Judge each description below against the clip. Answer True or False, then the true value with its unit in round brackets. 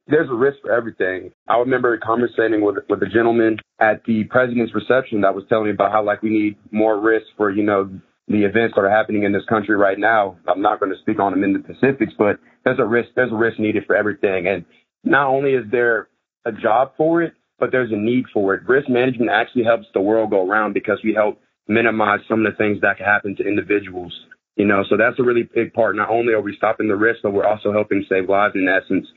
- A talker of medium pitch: False (110 Hz)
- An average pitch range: False (2.1 semitones)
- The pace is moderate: False (245 wpm)